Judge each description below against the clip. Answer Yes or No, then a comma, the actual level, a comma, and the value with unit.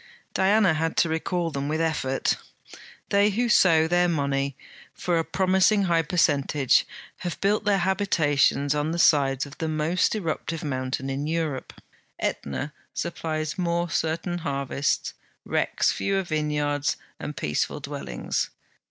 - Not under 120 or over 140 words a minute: Yes, slow, 135 wpm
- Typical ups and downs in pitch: Yes, average, 3.6 semitones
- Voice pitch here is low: No, medium, 160 Hz